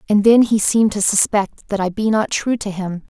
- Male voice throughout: No, female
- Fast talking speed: Yes, fast, 245 wpm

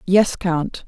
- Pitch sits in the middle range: Yes, medium, 180 Hz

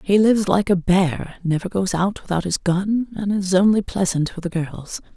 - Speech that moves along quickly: Yes, fast, 210 wpm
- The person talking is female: Yes, female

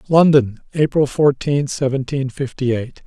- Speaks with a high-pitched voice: No, low, 135 Hz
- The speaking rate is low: Yes, slow, 115 wpm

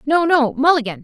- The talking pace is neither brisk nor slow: Yes, average, 175 wpm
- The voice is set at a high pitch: Yes, very high, 290 Hz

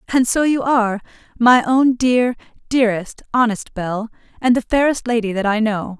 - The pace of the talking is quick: No, average, 150 wpm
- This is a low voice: No, high, 235 Hz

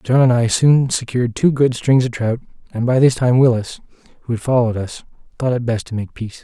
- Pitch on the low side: Yes, low, 120 Hz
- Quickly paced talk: Yes, fast, 235 wpm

